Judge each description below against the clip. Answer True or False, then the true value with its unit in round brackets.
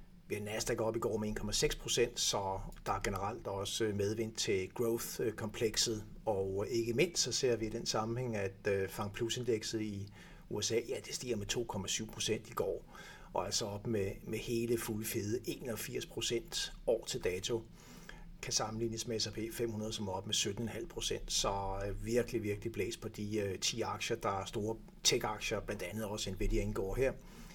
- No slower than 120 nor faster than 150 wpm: False (170 wpm)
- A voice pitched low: True (110 Hz)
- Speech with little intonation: True (2.1 semitones)